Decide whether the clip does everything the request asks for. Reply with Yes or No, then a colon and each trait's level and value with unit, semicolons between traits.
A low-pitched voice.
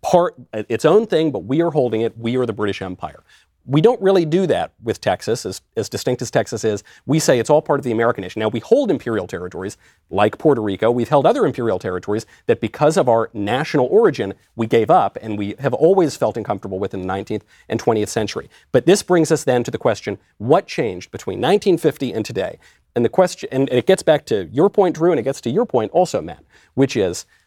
Yes: low, 125 Hz